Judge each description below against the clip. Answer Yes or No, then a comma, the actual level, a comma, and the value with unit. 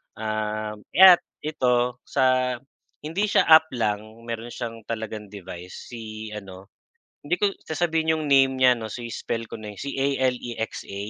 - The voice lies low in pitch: Yes, low, 120 Hz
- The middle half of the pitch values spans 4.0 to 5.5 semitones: Yes, average, 4.3 semitones